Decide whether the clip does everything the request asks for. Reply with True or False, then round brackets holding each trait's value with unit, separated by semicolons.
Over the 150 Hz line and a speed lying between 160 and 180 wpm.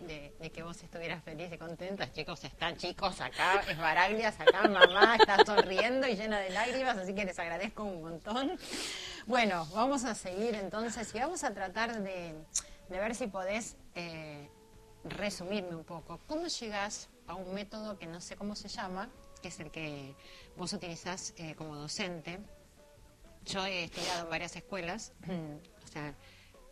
True (185 Hz; 165 wpm)